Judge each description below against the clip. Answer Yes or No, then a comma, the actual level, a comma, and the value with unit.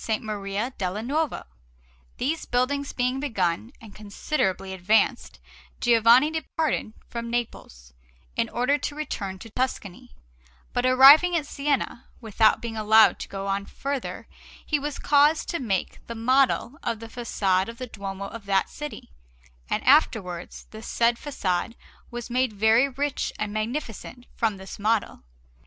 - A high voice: Yes, high, 230 Hz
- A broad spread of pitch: No, average, 4.7 semitones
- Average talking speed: Yes, average, 145 wpm